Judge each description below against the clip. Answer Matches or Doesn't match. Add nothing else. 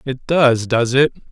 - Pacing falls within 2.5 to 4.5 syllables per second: Matches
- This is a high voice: Doesn't match